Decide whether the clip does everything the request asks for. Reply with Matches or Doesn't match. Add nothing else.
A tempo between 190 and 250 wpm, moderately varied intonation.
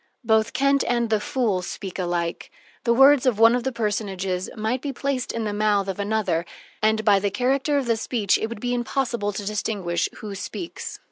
Matches